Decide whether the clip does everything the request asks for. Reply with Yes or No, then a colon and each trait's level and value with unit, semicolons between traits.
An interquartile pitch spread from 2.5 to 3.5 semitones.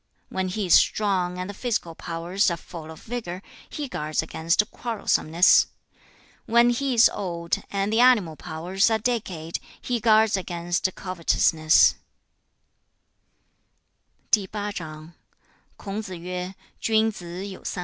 No: average, 4.6 semitones